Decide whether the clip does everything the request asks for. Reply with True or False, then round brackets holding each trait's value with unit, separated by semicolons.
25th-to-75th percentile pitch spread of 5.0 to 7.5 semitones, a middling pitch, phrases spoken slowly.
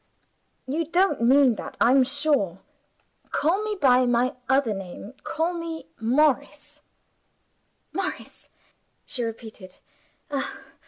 False (5.6 semitones; 265 Hz; 100 wpm)